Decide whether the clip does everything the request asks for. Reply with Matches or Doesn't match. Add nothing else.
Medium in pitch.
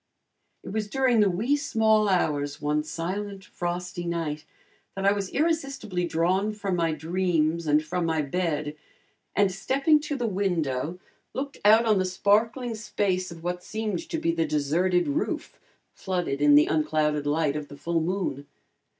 Matches